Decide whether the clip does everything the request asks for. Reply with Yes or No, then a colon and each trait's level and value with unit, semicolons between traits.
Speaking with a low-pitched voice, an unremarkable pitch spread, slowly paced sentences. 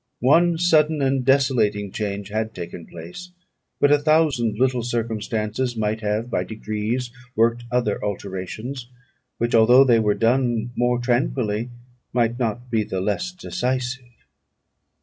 Yes: low, 120 Hz; average, 3.3 semitones; slow, 130 wpm